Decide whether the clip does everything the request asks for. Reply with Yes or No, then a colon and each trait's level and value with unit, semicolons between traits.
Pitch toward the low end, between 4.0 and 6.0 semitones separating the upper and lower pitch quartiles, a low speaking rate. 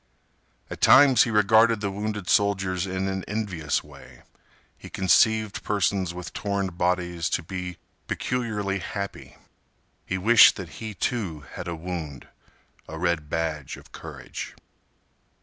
No: very low, 95 Hz; average, 3.3 semitones; slow, 130 wpm